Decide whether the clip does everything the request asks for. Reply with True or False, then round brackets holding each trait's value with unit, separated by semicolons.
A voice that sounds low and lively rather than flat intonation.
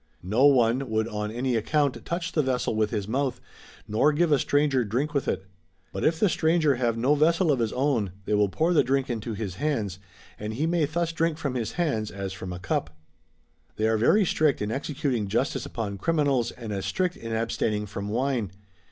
True (125 Hz; 5.7 semitones)